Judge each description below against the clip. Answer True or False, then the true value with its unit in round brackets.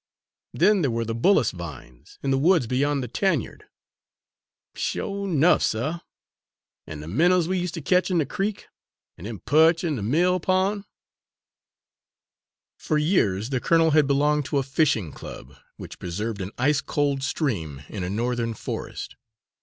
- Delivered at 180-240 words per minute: False (160 wpm)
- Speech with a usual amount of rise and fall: False (7.1 semitones)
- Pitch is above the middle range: False (140 Hz)